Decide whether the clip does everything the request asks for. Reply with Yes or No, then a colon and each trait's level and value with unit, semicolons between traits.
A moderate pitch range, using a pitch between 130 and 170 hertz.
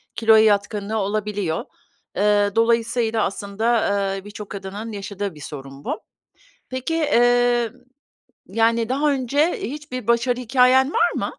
No: average, 3.4 semitones; high, 225 Hz